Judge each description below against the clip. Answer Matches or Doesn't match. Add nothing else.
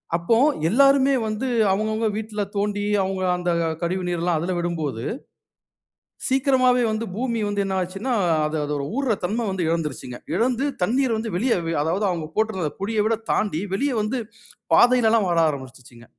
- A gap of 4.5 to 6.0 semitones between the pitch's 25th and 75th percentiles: Matches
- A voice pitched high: Matches